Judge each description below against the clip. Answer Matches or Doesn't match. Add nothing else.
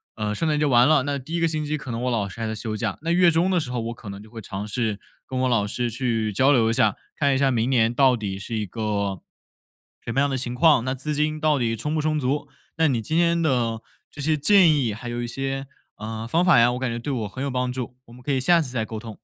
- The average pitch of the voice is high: Doesn't match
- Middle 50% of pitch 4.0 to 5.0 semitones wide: Matches